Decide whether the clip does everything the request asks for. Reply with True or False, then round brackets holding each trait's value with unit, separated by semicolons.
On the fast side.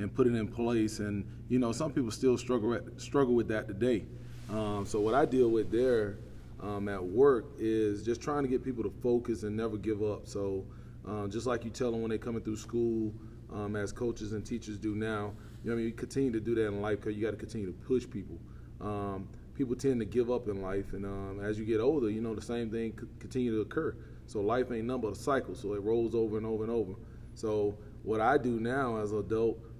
True (245 wpm)